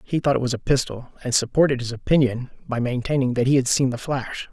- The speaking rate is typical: No, fast, 240 wpm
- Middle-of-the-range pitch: No, low, 130 Hz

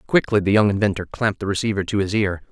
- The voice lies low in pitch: Yes, low, 100 Hz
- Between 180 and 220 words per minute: No, fast, 240 wpm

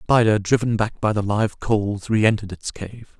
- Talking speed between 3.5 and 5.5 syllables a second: Yes, 5.1 syllables/s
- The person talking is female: No, male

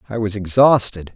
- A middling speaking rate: Yes, average, 155 wpm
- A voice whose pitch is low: Yes, low, 105 Hz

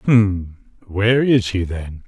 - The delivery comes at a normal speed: Yes, average, 145 wpm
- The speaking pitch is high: No, low, 100 Hz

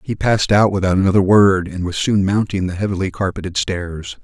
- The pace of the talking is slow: No, average, 200 wpm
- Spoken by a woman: No, male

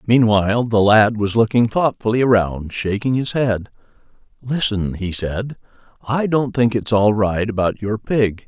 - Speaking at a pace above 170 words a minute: No, average, 155 wpm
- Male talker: Yes, male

